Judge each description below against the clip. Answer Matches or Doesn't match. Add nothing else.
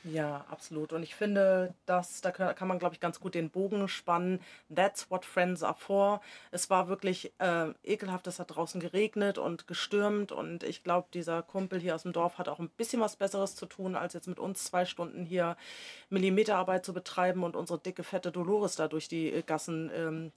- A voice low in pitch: Doesn't match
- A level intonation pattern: Matches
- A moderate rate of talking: Doesn't match